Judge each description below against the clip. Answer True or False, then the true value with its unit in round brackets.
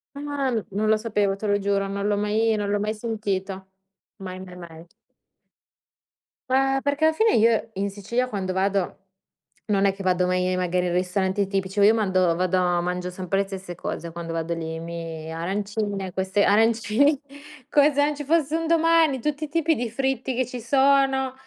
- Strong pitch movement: True (5.7 semitones)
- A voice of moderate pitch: False (205 Hz)